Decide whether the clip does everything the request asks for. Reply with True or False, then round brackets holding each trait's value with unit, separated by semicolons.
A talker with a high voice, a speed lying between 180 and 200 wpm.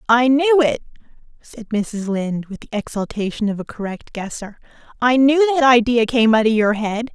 True (230 Hz; 185 wpm)